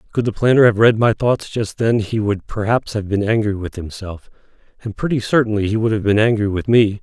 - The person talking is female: No, male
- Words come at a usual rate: No, fast, 230 wpm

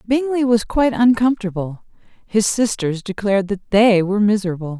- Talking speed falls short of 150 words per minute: Yes, average, 140 wpm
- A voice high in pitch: Yes, high, 210 Hz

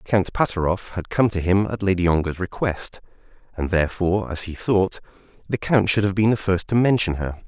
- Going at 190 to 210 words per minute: Yes, average, 200 wpm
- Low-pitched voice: Yes, very low, 95 Hz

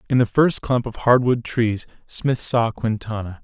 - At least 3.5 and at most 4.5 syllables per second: Yes, 4.3 syllables/s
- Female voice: No, male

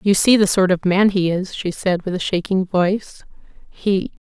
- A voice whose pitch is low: No, high, 190 Hz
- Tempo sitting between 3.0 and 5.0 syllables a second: Yes, 4.7 syllables/s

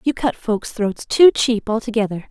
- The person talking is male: No, female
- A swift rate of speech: No, average, 180 wpm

